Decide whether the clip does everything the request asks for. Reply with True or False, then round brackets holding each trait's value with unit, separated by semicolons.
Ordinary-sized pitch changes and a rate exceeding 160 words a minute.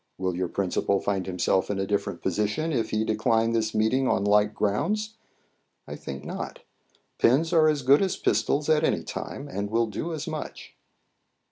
False (6.4 semitones; 175 wpm)